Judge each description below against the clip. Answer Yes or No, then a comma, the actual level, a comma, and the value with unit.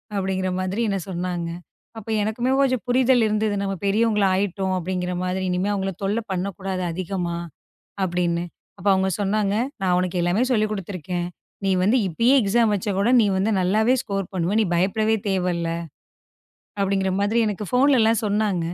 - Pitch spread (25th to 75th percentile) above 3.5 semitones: No, average, 2.8 semitones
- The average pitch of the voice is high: Yes, high, 195 Hz